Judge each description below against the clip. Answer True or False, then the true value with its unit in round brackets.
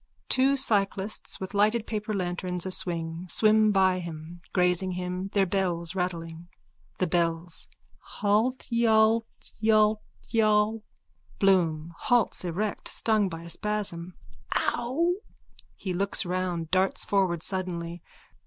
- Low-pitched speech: False (190 Hz)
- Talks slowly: True (105 wpm)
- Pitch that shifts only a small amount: False (3.6 semitones)